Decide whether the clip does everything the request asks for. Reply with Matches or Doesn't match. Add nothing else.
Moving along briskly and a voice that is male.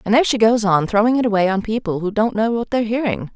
Doesn't match